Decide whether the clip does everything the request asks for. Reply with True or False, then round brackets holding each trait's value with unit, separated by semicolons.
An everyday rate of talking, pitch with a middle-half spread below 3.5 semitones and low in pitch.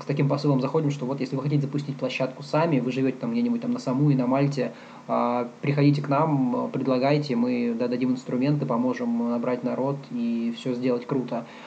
False (185 wpm; 2.5 semitones; 130 Hz)